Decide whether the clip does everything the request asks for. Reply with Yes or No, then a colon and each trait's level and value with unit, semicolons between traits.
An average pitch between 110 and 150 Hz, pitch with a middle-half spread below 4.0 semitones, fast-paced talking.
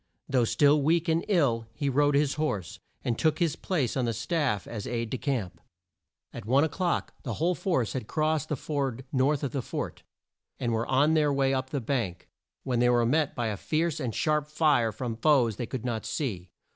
No: low, 135 Hz; average, 4.6 semitones; fast, 210 wpm